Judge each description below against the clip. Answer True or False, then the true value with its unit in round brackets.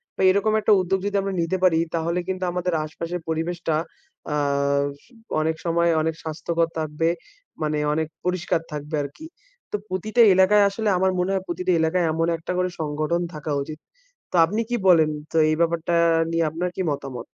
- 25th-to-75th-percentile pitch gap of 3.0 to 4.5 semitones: False (2.6 semitones)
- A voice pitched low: False (170 Hz)